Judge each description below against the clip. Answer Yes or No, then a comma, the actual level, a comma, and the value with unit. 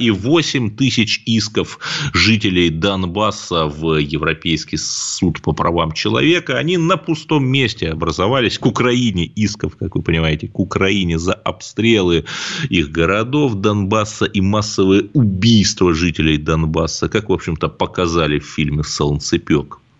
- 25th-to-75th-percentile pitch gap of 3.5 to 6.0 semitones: Yes, wide, 5.5 semitones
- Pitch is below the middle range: Yes, low, 100 Hz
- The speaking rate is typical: Yes, average, 125 wpm